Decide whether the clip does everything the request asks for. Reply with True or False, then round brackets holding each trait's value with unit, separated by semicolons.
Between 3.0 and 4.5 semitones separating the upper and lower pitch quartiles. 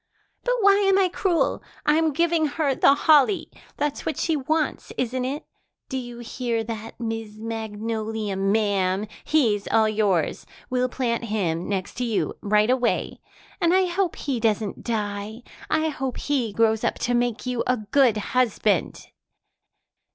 False (5.0 semitones)